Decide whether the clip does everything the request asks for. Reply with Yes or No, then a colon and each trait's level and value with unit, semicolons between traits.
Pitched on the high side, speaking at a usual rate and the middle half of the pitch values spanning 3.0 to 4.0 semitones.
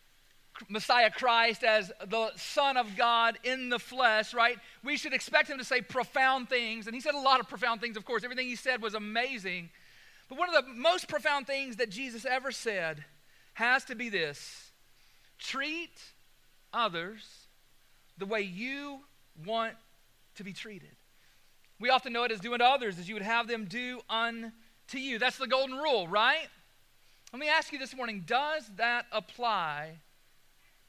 Yes: high, 235 Hz; average, 170 wpm; average, 3.6 semitones